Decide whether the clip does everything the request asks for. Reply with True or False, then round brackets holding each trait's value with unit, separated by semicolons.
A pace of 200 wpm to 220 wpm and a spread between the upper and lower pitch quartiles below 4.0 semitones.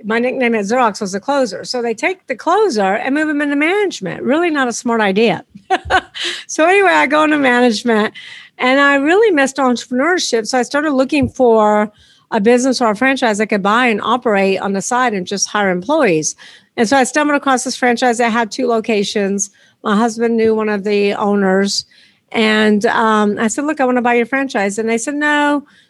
False (205 wpm; 4.3 semitones)